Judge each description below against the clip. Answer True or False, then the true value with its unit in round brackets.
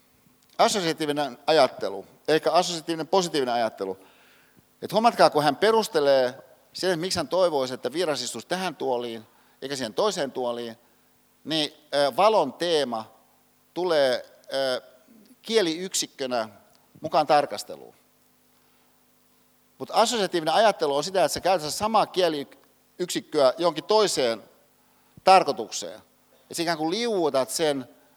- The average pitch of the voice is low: False (155 Hz)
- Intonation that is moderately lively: False (6.0 semitones)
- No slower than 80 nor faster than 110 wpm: True (100 wpm)